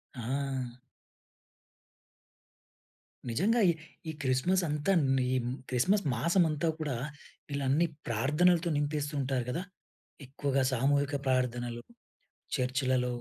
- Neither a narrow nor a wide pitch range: Yes, average, 3.2 semitones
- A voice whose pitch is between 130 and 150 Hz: Yes, low, 135 Hz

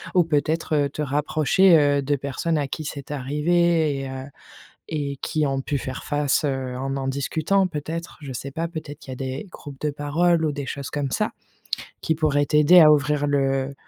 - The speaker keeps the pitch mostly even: Yes, narrow, 2.3 semitones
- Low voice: No, medium, 145 Hz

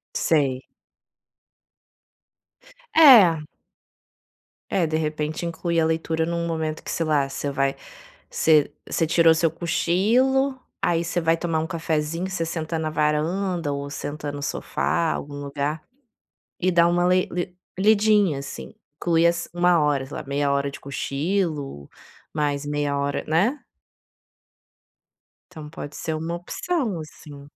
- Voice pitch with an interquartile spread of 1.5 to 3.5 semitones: Yes, average, 2.9 semitones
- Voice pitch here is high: No, medium, 160 Hz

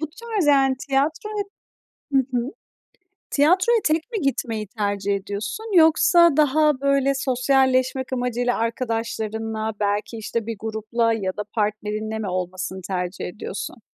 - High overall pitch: Yes, high, 240 Hz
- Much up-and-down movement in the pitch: No, average, 4.7 semitones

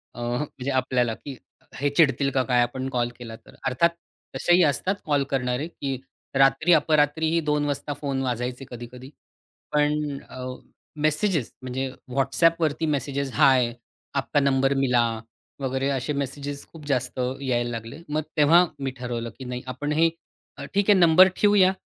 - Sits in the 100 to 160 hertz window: Yes, low, 135 Hz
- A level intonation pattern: No, average, 3.0 semitones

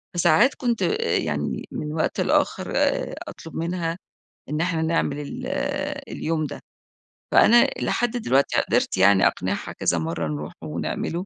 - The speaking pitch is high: No, medium, 155 Hz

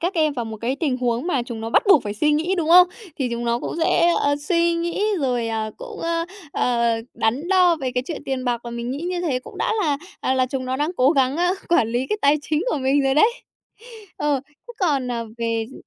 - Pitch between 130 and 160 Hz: No, very high, 275 Hz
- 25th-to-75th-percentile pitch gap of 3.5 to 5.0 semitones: No, wide, 5.6 semitones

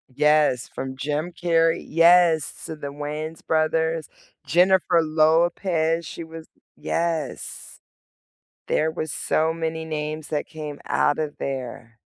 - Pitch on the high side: No, medium, 160 Hz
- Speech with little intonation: Yes, narrow, 1.6 semitones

